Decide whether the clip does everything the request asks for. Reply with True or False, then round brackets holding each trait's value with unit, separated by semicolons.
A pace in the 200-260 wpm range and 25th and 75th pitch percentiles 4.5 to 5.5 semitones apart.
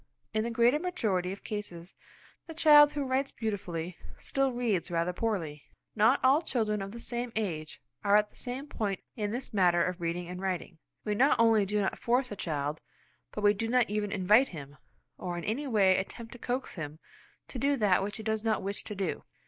True (205 wpm; 4.8 semitones)